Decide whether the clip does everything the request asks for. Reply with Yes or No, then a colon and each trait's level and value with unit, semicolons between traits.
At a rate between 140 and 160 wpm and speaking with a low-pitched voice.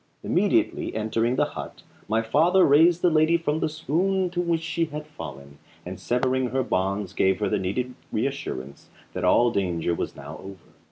No: average, 175 wpm; low, 125 Hz